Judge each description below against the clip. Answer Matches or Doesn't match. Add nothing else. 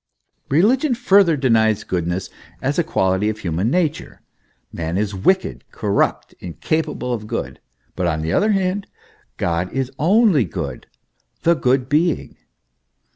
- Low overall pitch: Matches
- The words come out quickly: Doesn't match